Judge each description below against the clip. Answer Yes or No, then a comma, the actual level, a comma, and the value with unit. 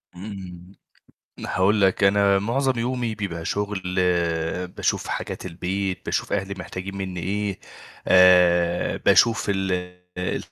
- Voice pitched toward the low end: Yes, very low, 95 Hz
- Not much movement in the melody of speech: Yes, narrow, 2.1 semitones